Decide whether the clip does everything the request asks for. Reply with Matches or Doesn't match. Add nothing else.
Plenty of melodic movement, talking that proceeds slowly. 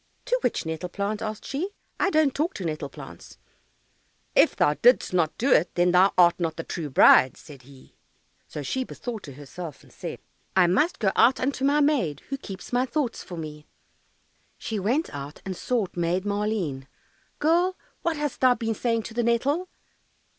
Doesn't match